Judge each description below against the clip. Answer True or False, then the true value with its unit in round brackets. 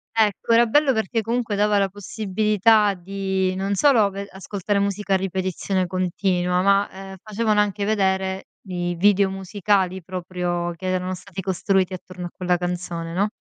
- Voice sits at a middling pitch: False (195 Hz)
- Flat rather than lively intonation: True (2.0 semitones)